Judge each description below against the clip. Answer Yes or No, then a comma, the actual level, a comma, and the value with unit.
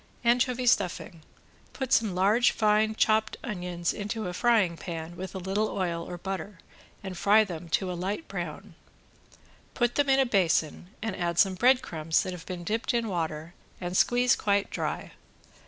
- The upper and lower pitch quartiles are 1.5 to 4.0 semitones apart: No, average, 4.4 semitones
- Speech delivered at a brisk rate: No, average, 170 wpm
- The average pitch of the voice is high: Yes, high, 195 Hz